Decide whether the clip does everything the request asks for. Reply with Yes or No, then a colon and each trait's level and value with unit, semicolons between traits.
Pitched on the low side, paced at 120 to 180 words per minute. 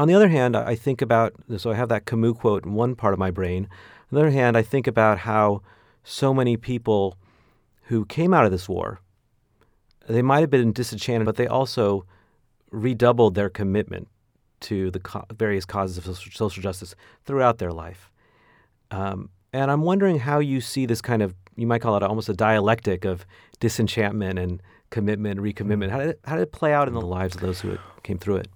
No: low, 110 Hz; average, 200 wpm